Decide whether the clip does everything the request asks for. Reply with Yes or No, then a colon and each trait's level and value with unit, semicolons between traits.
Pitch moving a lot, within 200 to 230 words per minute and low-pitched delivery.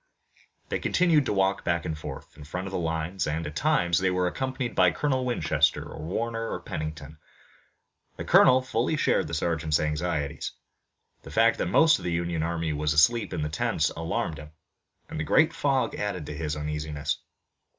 No: wide, 6.6 semitones; average, 185 wpm; very low, 85 Hz